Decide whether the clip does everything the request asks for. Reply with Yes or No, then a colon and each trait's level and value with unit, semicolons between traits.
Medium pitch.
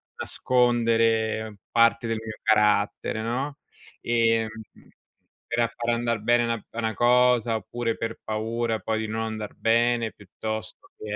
No: low, 115 Hz